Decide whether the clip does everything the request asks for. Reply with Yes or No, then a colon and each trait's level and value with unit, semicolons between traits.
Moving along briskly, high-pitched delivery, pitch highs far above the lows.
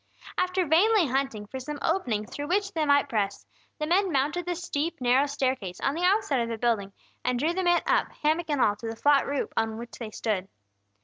Yes: fast, 220 wpm; very high, 285 Hz; wide, 6.7 semitones